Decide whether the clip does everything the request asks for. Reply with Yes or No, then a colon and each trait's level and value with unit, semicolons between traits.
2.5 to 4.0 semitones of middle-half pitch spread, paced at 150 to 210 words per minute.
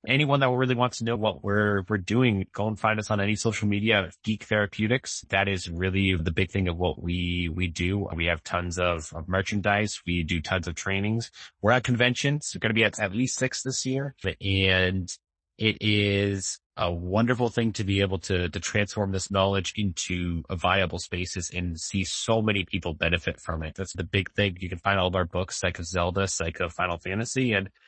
Yes: average, 3.3 semitones; fast, 205 wpm